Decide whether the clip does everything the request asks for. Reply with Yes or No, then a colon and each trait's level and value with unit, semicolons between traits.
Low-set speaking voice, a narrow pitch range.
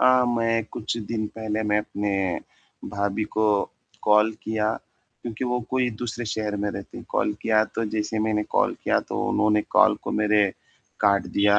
Yes: low, 110 Hz; narrow, 1.5 semitones